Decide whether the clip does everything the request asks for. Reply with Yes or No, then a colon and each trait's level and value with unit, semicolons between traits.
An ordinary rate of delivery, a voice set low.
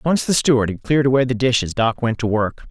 No: fast, 265 wpm; low, 120 Hz